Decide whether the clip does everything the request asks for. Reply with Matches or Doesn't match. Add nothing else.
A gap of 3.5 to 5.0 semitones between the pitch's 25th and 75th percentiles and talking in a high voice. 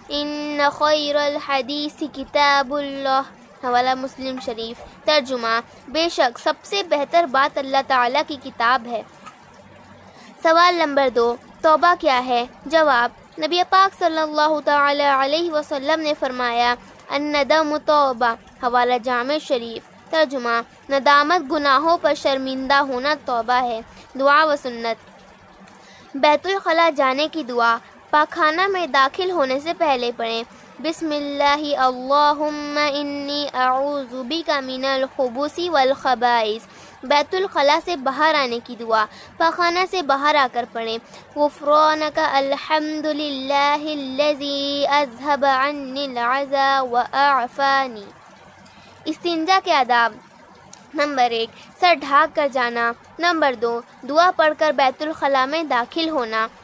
Doesn't match